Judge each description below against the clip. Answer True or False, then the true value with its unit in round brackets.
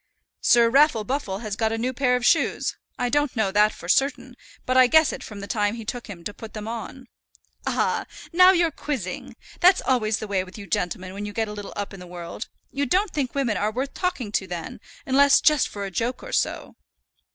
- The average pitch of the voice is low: False (230 Hz)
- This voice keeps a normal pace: False (230 wpm)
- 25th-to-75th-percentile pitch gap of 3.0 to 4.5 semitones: False (5.1 semitones)